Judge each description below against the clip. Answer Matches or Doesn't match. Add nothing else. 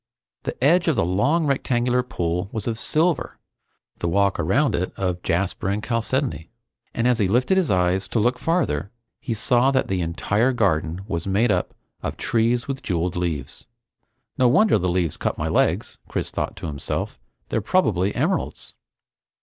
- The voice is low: Matches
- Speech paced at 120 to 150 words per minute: Doesn't match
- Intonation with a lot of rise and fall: Matches